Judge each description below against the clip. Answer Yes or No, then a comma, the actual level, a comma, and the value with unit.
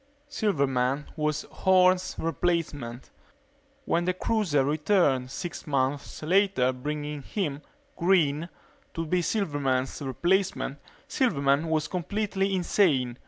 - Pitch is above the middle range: No, medium, 155 Hz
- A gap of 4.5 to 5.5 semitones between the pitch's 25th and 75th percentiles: Yes, average, 5.0 semitones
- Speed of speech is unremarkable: No, slow, 100 wpm